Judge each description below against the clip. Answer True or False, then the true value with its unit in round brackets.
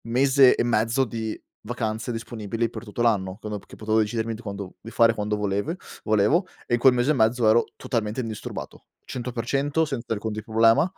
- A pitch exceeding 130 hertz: False (115 Hz)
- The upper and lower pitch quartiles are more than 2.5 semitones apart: False (2.1 semitones)